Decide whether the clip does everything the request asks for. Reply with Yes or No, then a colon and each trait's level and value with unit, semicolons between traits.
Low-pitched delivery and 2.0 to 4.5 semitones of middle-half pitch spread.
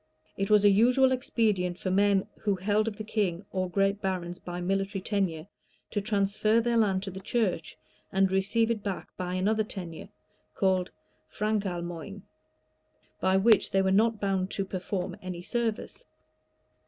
No: high, 195 Hz; narrow, 2.4 semitones